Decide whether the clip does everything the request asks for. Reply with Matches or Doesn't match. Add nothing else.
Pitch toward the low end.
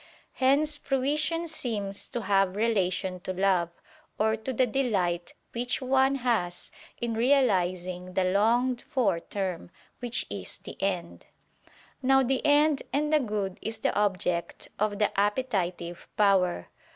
Doesn't match